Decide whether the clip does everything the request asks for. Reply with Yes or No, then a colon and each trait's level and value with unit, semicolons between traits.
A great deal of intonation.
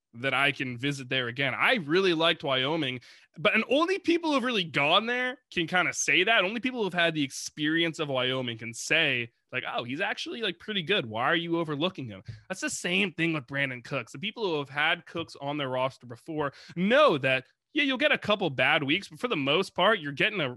Yes: wide, 6.7 semitones